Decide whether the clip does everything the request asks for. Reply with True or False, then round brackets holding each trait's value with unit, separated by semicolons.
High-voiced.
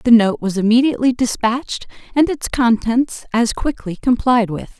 True (240 Hz)